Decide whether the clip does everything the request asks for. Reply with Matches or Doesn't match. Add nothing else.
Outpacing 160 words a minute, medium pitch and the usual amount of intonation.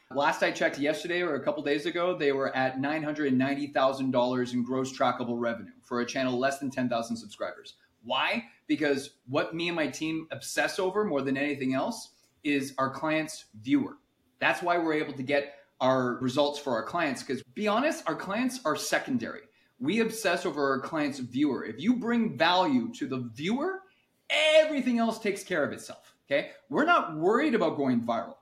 Doesn't match